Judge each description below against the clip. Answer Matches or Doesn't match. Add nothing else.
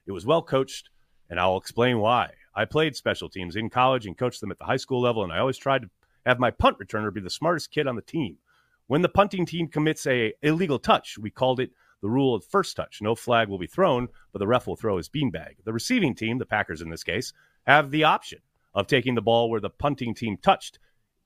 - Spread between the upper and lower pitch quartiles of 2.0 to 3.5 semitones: Doesn't match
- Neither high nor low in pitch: Doesn't match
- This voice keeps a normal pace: Doesn't match